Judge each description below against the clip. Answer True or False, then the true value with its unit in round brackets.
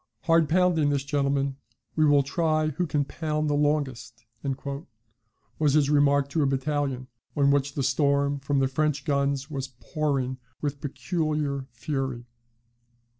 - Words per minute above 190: False (140 wpm)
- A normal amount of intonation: False (1.8 semitones)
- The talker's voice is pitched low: False (145 Hz)